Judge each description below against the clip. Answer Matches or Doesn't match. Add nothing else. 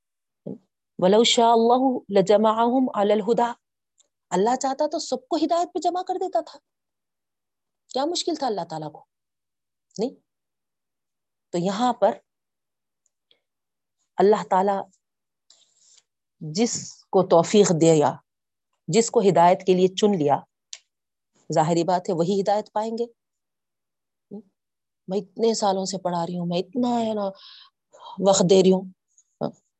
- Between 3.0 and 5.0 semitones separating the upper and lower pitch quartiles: Matches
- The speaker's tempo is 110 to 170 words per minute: Matches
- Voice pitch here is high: Matches